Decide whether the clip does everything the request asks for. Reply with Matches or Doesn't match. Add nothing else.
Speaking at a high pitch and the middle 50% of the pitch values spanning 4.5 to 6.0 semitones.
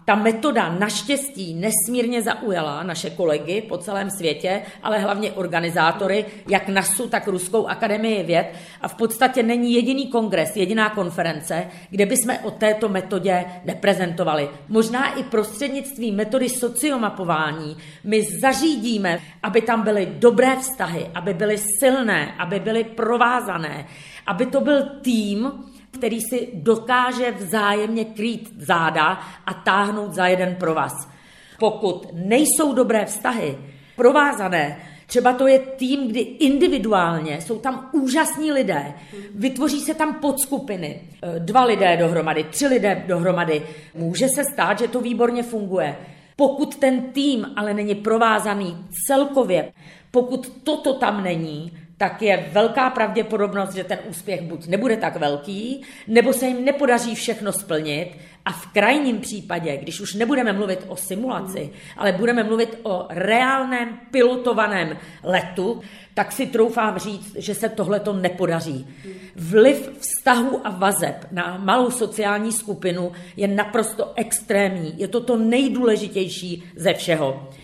Matches